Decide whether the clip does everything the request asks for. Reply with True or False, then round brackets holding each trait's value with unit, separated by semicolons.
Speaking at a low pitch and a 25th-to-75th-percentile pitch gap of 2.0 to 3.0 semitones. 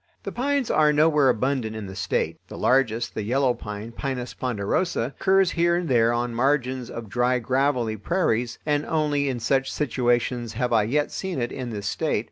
False (125 Hz; 4.0 semitones)